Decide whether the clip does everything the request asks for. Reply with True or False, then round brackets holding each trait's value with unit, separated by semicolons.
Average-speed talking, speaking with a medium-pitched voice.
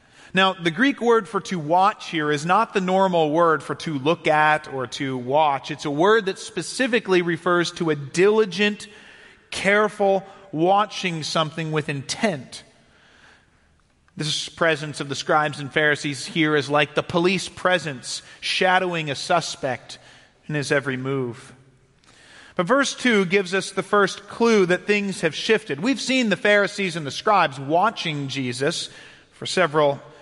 True (155 wpm; 170 Hz)